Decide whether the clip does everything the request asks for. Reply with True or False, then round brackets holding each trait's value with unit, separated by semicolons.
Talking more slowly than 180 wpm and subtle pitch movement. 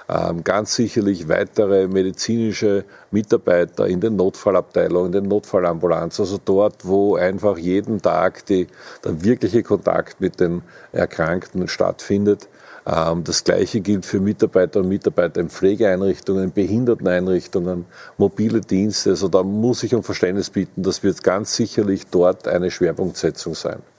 True (130 wpm; 2.2 semitones)